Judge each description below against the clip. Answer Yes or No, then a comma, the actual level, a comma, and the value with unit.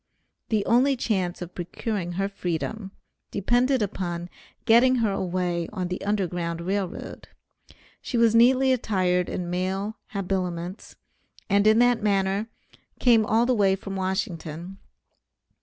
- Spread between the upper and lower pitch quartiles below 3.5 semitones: No, average, 3.8 semitones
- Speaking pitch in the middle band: No, high, 195 Hz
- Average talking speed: No, slow, 130 wpm